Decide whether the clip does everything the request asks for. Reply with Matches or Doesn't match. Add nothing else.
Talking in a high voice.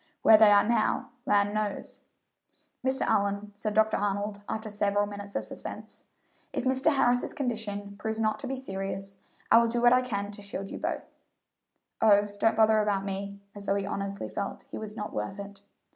Matches